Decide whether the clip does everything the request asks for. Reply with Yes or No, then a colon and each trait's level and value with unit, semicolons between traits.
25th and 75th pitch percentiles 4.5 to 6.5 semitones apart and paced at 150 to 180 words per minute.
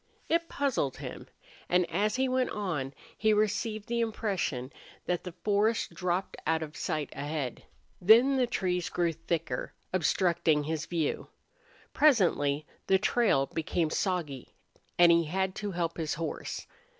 No: average, 5.1 semitones; average, 140 wpm